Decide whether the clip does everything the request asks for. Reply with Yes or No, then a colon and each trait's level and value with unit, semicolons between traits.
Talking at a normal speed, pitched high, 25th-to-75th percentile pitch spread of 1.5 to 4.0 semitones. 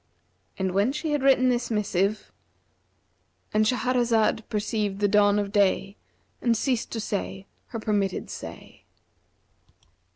No: slow, 120 wpm; high, 215 Hz; average, 2.9 semitones